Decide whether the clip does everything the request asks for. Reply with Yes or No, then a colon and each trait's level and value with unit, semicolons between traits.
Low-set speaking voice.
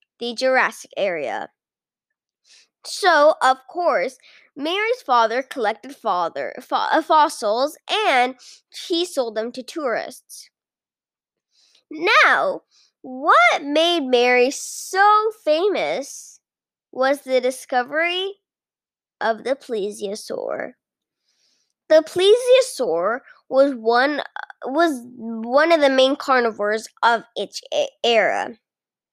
No: very high, 280 Hz